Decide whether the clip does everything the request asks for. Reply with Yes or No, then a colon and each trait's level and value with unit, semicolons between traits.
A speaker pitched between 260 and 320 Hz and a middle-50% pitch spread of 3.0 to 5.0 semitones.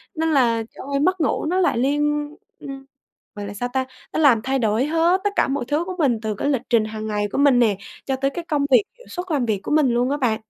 Yes: very high, 270 Hz; average, 4.5 semitones